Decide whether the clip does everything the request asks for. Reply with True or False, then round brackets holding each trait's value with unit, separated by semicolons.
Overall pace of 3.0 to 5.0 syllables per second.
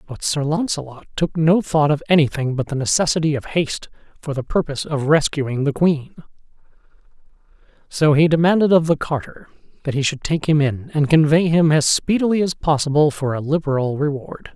False (5.5 syllables/s)